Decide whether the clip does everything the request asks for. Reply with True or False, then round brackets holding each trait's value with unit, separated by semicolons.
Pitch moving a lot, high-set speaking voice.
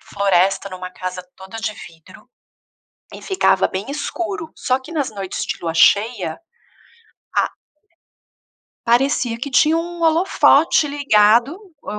True (7.8 semitones; 235 Hz)